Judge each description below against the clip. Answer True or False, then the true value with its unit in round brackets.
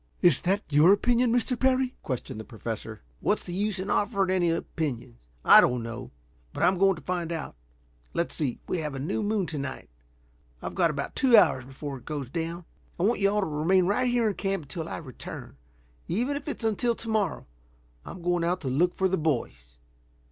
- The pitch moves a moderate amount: False (6.2 semitones)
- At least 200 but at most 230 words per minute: True (205 wpm)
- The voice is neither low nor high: True (175 Hz)